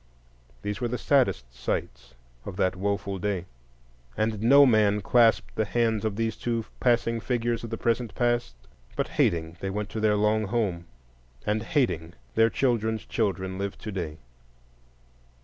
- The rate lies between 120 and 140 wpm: No, average, 150 wpm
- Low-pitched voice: Yes, low, 110 Hz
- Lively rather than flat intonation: No, average, 3.2 semitones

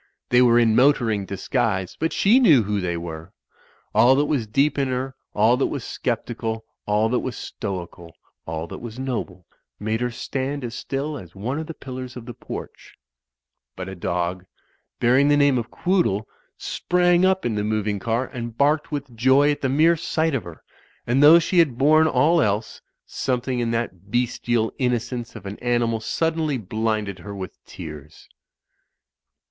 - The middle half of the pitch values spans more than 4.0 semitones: Yes, average, 5.0 semitones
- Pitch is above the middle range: No, low, 120 Hz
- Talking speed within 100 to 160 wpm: No, average, 175 wpm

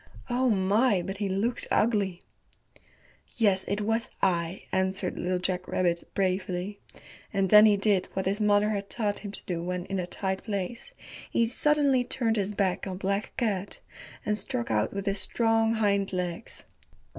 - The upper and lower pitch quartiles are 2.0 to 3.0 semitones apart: Yes, narrow, 2.5 semitones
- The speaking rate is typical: Yes, average, 170 wpm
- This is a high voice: Yes, high, 200 Hz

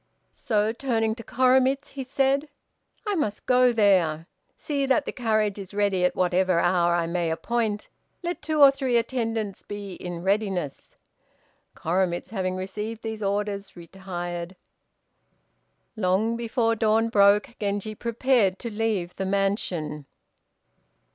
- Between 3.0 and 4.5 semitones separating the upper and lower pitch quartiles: Yes, average, 4.0 semitones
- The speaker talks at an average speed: No, slow, 130 wpm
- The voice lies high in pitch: Yes, high, 210 Hz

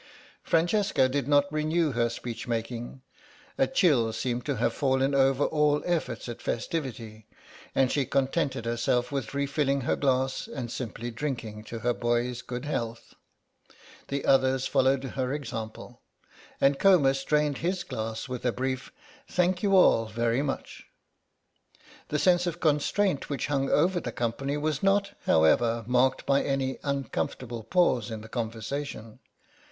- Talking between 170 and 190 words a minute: No, average, 145 wpm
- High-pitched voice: No, low, 135 Hz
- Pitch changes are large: No, average, 3.7 semitones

